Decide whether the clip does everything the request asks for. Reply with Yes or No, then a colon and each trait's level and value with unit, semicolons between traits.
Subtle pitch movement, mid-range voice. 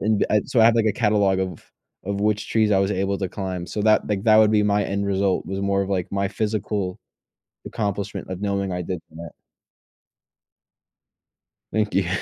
No: narrow, 1.7 semitones; low, 100 Hz